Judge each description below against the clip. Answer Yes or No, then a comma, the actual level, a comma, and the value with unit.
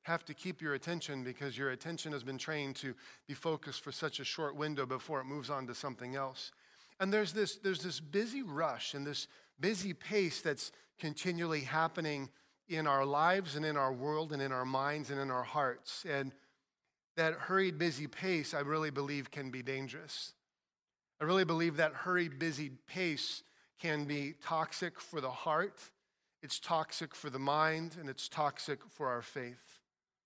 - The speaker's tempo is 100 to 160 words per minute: No, average, 180 wpm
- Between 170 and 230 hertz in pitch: No, medium, 150 Hz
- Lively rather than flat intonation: No, average, 3.2 semitones